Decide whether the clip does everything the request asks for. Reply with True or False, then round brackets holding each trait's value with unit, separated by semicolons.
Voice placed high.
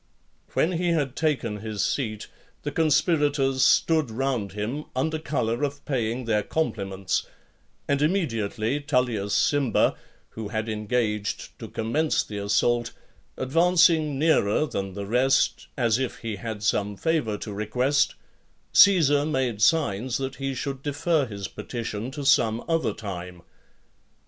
False (125 Hz)